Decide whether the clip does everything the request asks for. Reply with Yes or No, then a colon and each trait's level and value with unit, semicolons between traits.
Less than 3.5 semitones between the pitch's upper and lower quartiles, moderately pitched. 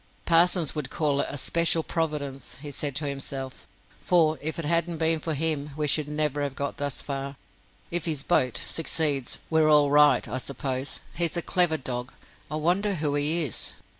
Yes: narrow, 2.6 semitones; medium, 150 Hz